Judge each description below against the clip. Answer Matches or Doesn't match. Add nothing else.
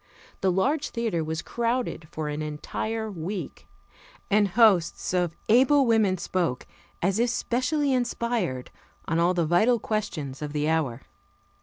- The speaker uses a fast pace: Doesn't match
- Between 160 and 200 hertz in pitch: Matches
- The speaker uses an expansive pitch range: Matches